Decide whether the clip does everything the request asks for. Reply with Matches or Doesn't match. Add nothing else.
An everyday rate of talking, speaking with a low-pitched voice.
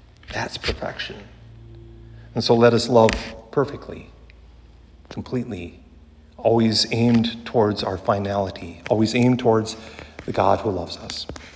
Doesn't match